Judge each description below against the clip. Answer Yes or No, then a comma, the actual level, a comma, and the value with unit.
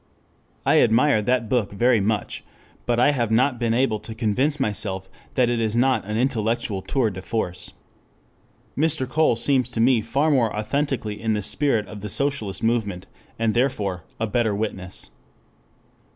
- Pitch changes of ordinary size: Yes, average, 3.4 semitones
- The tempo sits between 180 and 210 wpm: No, average, 165 wpm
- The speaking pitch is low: Yes, low, 115 Hz